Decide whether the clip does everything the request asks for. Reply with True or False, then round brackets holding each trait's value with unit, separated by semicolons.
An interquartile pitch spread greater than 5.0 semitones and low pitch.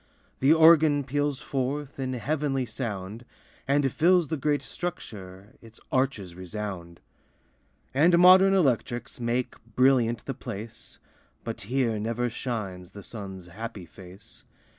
True (5.6 semitones; 125 Hz)